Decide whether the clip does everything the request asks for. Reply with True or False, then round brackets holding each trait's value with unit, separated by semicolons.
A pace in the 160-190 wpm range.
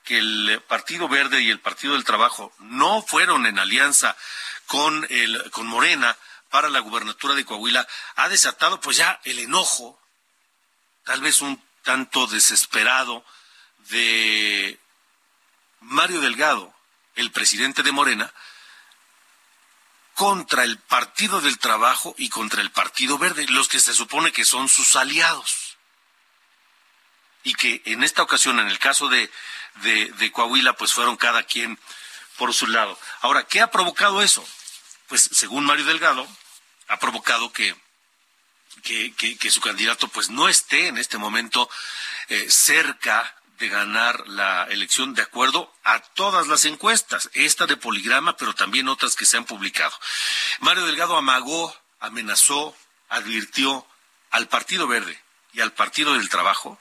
False (145 wpm)